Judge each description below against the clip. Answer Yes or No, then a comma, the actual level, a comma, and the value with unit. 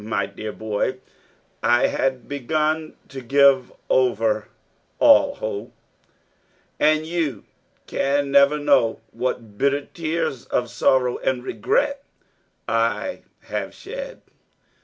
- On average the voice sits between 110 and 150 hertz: Yes, low, 135 Hz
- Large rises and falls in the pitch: No, average, 4.6 semitones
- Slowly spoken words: Yes, slow, 105 wpm